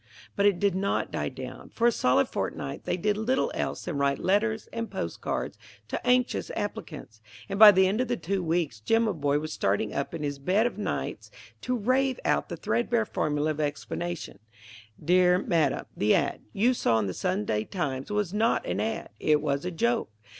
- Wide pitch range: Yes, wide, 6.9 semitones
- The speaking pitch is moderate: Yes, medium, 180 Hz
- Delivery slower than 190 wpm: No, average, 195 wpm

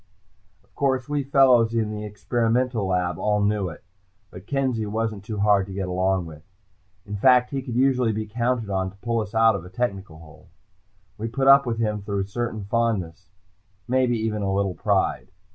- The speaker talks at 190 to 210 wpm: Yes, average, 195 wpm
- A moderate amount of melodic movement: Yes, average, 3.7 semitones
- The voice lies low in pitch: Yes, low, 110 Hz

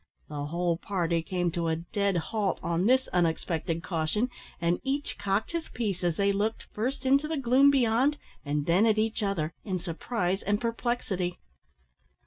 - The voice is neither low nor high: No, high, 195 Hz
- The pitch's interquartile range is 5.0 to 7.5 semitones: Yes, wide, 5.4 semitones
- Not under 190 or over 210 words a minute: No, average, 165 wpm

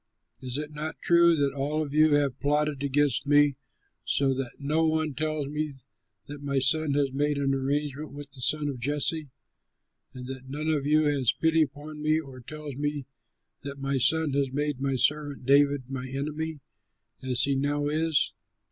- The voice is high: No, medium, 145 Hz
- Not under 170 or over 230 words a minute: Yes, average, 180 wpm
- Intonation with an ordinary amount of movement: No, narrow, 1.9 semitones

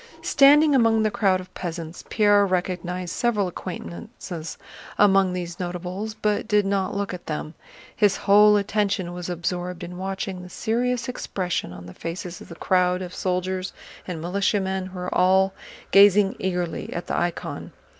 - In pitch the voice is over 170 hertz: Yes, medium, 185 Hz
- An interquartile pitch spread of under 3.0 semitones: Yes, narrow, 2.4 semitones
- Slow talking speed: No, average, 155 wpm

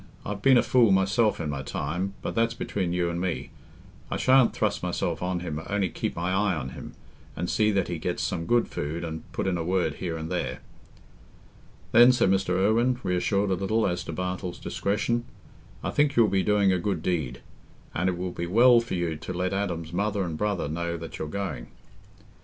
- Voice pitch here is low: Yes, very low, 95 Hz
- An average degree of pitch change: Yes, average, 3.4 semitones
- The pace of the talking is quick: Yes, fast, 210 wpm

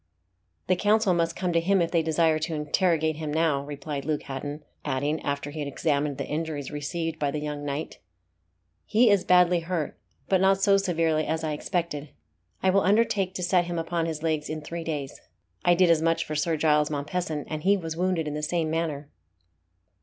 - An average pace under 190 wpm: No, average, 200 wpm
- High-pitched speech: No, medium, 160 Hz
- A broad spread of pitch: No, average, 2.8 semitones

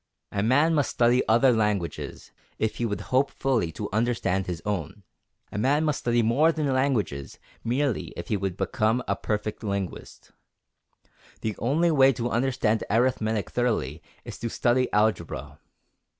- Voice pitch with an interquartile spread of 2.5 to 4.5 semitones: Yes, average, 4.0 semitones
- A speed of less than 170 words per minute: Yes, average, 150 wpm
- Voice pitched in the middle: No, low, 115 Hz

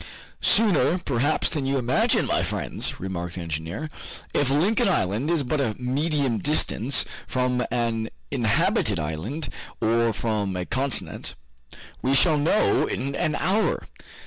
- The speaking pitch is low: Yes, low, 130 Hz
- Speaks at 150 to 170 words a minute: No, slow, 135 wpm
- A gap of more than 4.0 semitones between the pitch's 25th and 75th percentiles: Yes, wide, 5.4 semitones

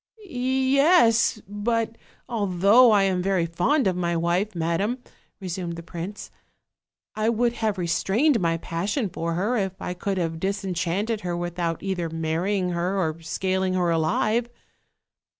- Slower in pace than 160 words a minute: Yes, average, 140 wpm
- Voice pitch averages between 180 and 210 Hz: Yes, high, 190 Hz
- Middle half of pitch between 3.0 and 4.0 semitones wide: No, average, 4.4 semitones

